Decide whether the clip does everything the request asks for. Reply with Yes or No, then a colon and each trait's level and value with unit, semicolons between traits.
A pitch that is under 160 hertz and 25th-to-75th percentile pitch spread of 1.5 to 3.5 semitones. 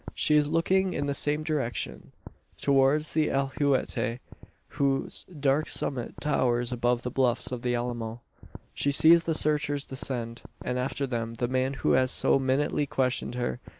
Yes: low, 135 Hz; average, 3.1 semitones